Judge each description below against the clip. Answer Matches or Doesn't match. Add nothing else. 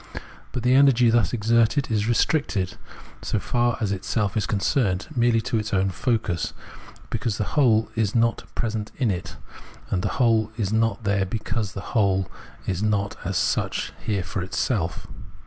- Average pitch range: Matches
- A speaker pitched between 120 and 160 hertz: Doesn't match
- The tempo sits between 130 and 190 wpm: Matches